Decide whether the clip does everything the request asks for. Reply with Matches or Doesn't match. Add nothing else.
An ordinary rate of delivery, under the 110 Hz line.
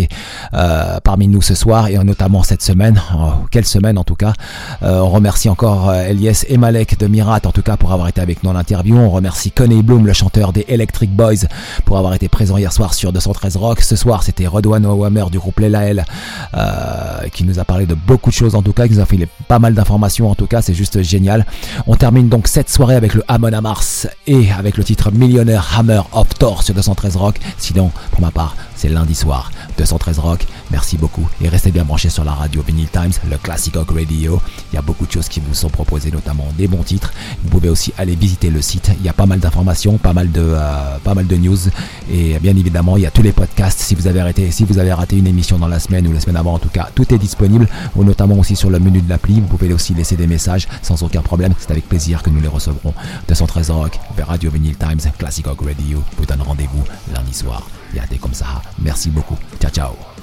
Doesn't match